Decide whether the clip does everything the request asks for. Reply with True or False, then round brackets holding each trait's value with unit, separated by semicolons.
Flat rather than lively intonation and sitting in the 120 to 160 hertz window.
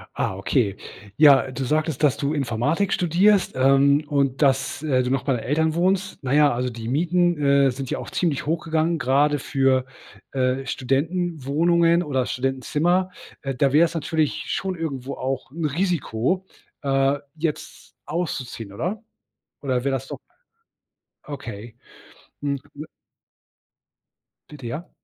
False (3.8 semitones; 140 Hz)